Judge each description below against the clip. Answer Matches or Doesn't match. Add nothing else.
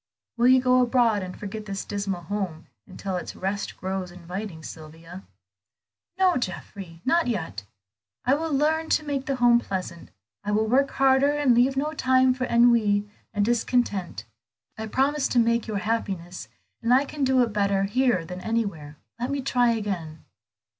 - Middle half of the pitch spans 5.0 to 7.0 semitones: Matches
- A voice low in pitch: Doesn't match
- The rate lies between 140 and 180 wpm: Matches